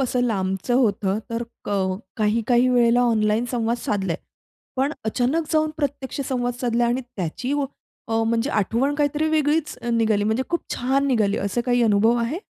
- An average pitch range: Yes, average, 3.5 semitones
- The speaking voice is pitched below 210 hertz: No, high, 240 Hz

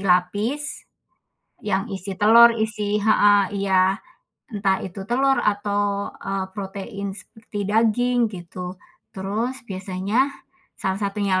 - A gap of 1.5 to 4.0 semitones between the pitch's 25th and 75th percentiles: Yes, narrow, 2.4 semitones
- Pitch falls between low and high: No, high, 205 Hz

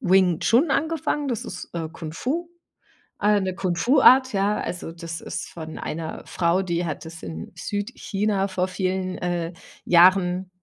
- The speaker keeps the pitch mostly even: No, average, 3.4 semitones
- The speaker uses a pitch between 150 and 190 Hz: Yes, medium, 185 Hz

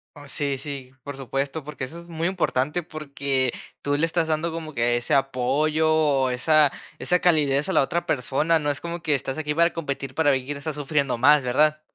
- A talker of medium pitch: Yes, medium, 145 Hz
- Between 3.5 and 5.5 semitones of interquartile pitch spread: No, average, 2.7 semitones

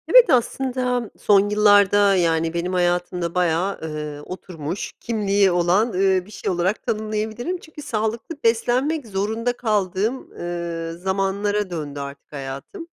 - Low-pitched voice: No, high, 195 Hz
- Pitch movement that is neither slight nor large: Yes, average, 4.2 semitones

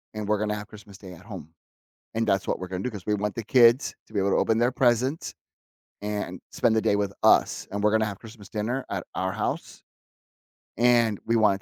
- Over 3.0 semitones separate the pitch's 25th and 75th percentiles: No, narrow, 2.6 semitones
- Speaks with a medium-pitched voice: No, low, 105 Hz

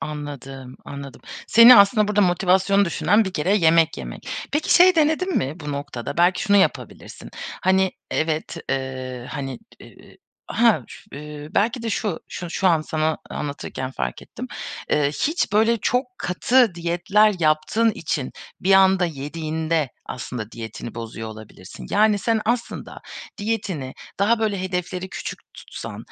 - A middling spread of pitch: No, wide, 6.6 semitones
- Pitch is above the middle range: No, medium, 175 Hz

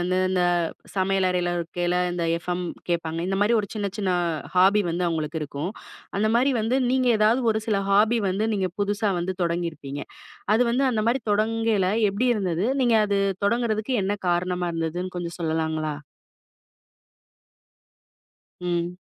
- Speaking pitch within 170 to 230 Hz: Yes, medium, 185 Hz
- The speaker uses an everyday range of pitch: Yes, average, 3.8 semitones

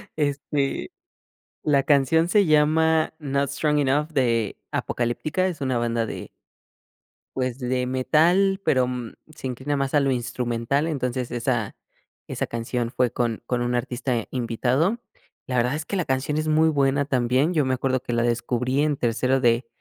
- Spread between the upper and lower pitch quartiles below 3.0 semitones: No, average, 3.4 semitones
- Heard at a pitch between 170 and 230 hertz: No, low, 130 Hz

